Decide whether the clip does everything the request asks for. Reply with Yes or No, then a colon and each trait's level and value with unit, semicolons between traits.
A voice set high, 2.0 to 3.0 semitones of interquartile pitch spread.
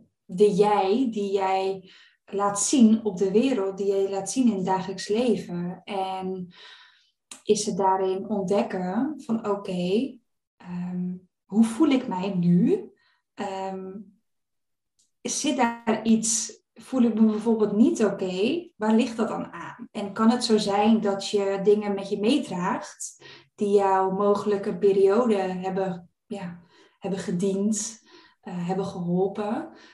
Yes: high, 205 Hz; narrow, 2.6 semitones